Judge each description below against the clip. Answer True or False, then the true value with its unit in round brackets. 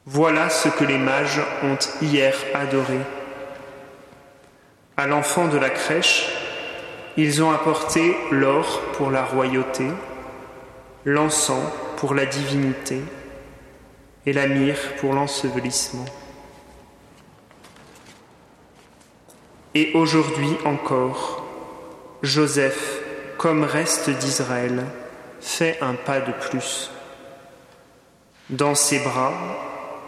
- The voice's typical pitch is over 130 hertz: True (140 Hz)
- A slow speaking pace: True (90 wpm)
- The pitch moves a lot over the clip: False (1.8 semitones)